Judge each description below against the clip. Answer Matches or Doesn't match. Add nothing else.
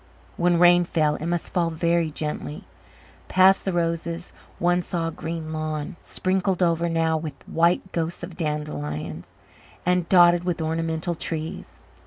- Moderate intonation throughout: Doesn't match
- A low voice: Doesn't match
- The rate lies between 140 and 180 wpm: Matches